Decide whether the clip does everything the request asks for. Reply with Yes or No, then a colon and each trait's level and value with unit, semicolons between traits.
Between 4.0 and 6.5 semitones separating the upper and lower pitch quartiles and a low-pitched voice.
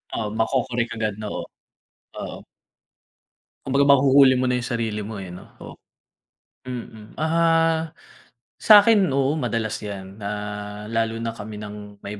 Yes: average, 4.6 semitones; low, 115 Hz